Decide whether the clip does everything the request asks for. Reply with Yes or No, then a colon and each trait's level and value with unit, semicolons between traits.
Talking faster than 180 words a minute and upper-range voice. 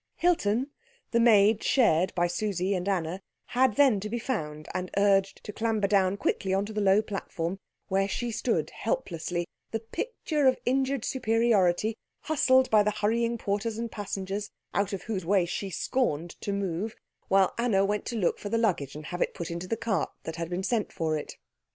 Yes: average, 190 wpm; high, 200 Hz